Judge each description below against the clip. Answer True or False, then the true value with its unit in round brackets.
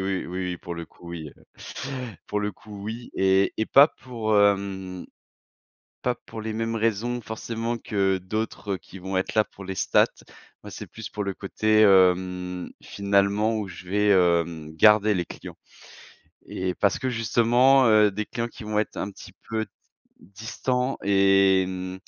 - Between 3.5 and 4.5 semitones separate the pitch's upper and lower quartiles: False (2.9 semitones)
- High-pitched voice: False (100 Hz)